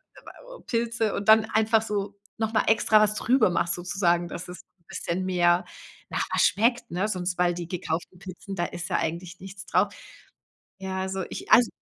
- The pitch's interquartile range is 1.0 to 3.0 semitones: No, average, 3.6 semitones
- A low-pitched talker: No, high, 190 Hz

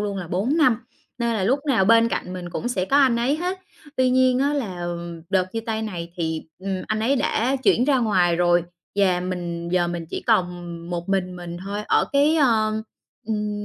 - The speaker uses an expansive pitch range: Yes, wide, 5.8 semitones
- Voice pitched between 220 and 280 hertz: No, high, 205 Hz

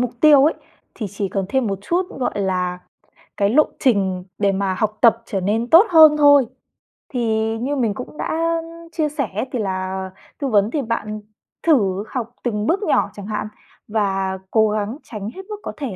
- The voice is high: Yes, high, 225 Hz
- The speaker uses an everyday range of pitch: No, wide, 6.1 semitones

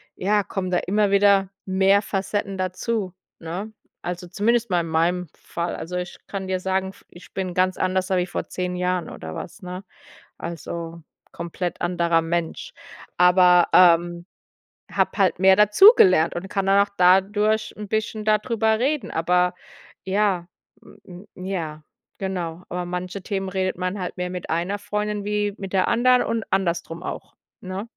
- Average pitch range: No, narrow, 2.3 semitones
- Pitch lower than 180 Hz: No, medium, 185 Hz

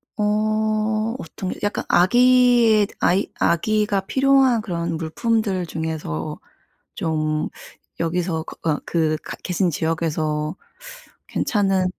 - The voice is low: No, high, 190 Hz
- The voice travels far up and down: No, average, 5.0 semitones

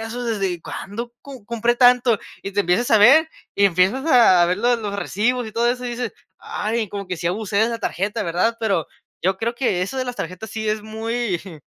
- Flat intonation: No, average, 3.6 semitones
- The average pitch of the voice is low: No, high, 220 Hz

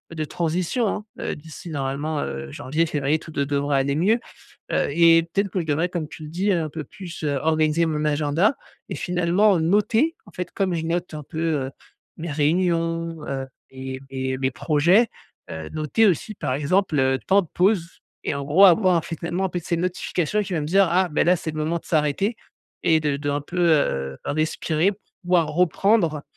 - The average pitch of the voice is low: No, medium, 165 Hz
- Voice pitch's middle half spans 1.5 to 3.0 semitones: No, average, 3.6 semitones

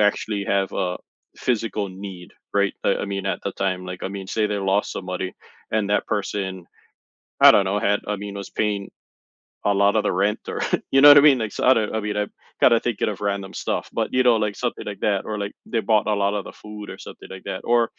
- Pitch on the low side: Yes, low, 100 Hz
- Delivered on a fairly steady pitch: Yes, narrow, 1.6 semitones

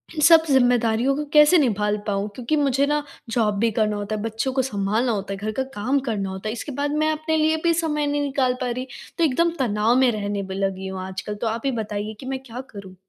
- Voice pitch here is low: No, high, 240 Hz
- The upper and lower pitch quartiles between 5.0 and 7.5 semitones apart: Yes, wide, 5.4 semitones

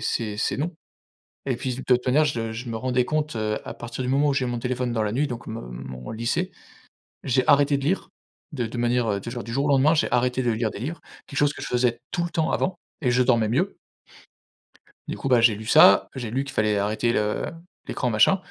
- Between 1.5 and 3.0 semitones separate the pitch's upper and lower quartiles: No, average, 3.4 semitones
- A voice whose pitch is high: No, low, 125 Hz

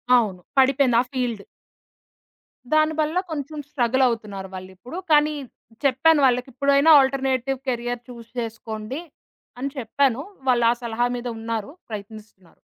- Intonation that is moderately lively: Yes, average, 3.6 semitones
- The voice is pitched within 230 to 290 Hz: Yes, high, 245 Hz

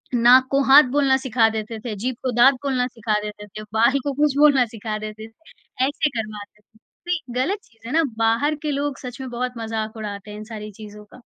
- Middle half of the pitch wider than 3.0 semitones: Yes, average, 4.0 semitones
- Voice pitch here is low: No, high, 235 Hz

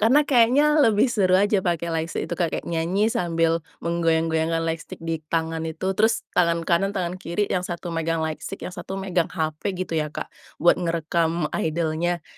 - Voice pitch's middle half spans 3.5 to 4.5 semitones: No, average, 2.7 semitones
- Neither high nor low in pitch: Yes, medium, 170 Hz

